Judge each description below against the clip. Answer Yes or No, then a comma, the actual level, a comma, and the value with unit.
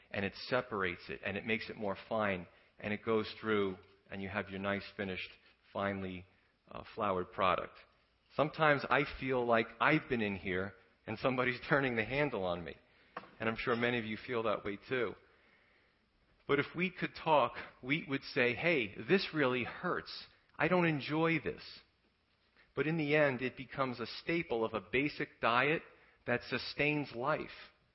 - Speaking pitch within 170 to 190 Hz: No, low, 120 Hz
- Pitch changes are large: Yes, wide, 6.1 semitones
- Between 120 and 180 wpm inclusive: Yes, average, 170 wpm